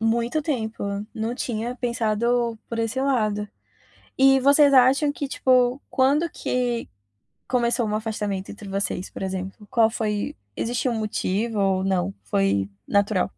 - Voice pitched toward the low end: No, high, 230 Hz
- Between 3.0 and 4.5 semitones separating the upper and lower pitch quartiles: Yes, average, 3.5 semitones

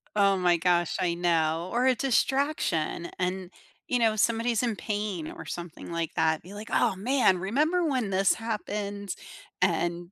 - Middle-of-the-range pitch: No, high, 195 Hz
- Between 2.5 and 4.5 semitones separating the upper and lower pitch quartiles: No, average, 4.9 semitones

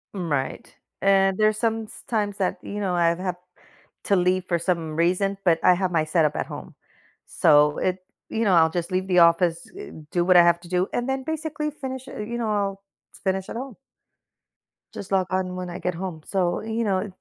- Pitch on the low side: No, medium, 185 Hz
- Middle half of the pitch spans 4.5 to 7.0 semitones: No, average, 3.3 semitones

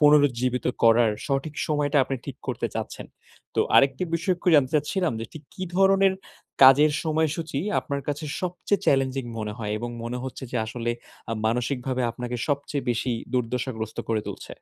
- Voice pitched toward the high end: No, low, 135 Hz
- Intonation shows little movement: No, average, 3.7 semitones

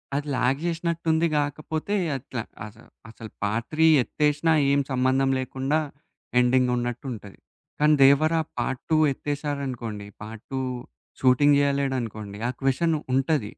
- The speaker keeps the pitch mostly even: No, average, 3.4 semitones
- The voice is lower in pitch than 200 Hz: Yes, low, 135 Hz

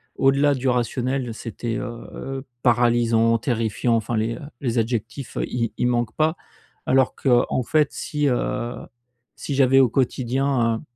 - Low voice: Yes, low, 125 Hz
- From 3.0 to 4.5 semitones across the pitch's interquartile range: No, narrow, 2.5 semitones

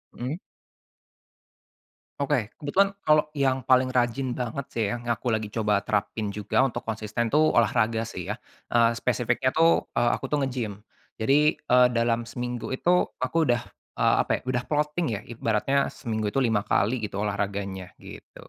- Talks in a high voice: No, low, 120 Hz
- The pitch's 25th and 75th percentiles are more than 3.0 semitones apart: Yes, average, 3.5 semitones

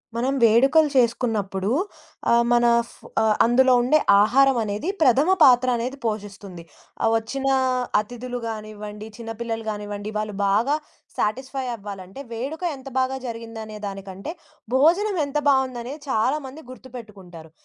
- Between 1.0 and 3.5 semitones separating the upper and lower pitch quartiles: No, average, 3.9 semitones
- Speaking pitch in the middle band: No, high, 235 Hz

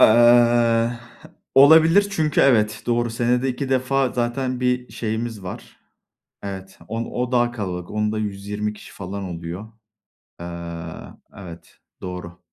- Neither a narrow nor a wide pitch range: Yes, average, 4.0 semitones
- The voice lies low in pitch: Yes, low, 115 Hz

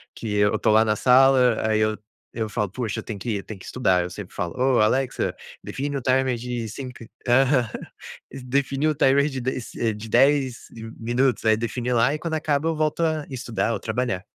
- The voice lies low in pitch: Yes, low, 125 Hz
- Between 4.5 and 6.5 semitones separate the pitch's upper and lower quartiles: No, average, 3.5 semitones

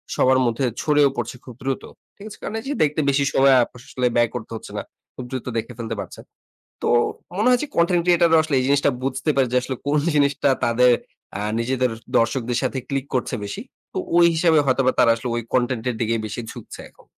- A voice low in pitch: Yes, low, 130 Hz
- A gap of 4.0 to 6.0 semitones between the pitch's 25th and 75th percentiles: No, average, 3.3 semitones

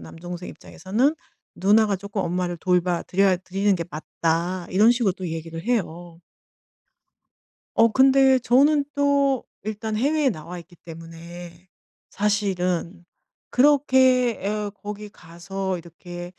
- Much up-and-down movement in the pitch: No, average, 4.9 semitones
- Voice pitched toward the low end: No, high, 190 Hz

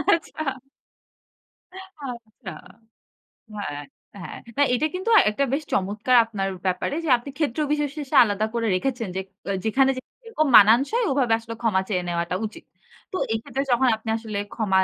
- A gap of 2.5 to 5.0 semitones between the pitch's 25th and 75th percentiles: No, wide, 5.6 semitones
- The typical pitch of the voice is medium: No, high, 235 Hz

